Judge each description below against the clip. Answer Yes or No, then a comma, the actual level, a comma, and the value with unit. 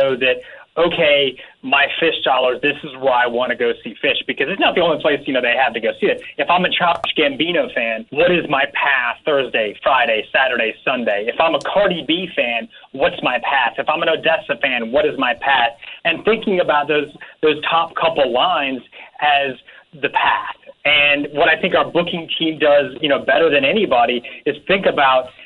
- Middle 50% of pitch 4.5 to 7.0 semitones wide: Yes, average, 4.9 semitones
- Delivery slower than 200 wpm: No, fast, 205 wpm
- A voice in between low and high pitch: Yes, medium, 150 Hz